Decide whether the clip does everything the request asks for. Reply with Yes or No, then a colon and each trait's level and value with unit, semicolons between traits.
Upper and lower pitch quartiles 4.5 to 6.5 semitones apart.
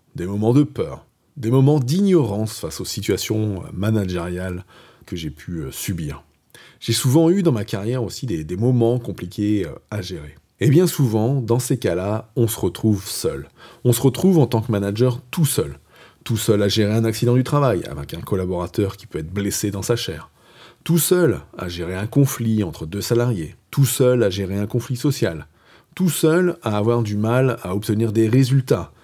Yes: average, 4.8 semitones